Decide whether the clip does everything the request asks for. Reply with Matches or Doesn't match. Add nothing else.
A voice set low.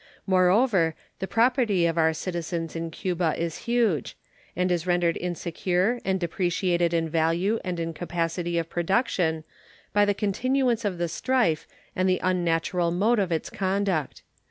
Doesn't match